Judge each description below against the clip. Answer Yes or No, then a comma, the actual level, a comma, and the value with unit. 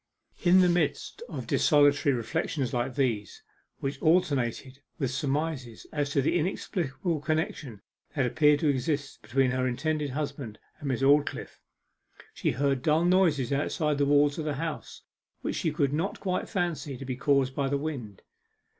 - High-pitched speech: No, medium, 145 Hz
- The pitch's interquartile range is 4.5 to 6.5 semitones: No, average, 2.9 semitones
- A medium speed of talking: Yes, average, 160 wpm